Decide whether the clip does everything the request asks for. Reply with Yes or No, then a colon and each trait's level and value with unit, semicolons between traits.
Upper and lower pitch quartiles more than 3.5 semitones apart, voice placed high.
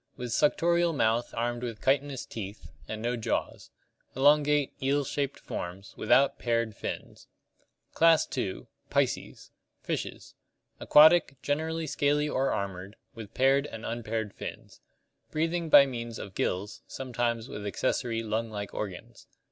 No: average, 4.6 semitones; low, 120 Hz